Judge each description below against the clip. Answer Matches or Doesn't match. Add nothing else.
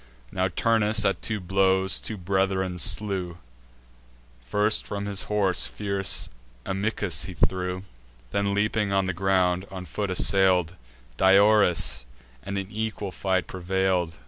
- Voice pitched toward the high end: Doesn't match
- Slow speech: Matches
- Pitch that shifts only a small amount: Matches